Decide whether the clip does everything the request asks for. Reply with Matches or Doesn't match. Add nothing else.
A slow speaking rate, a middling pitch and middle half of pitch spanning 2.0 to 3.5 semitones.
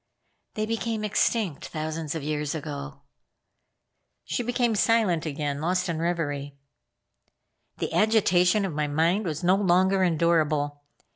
Doesn't match